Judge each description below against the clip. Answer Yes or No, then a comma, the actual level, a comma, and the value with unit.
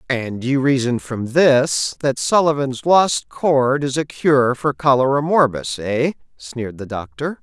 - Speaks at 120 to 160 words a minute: Yes, average, 155 wpm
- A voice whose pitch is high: No, low, 135 Hz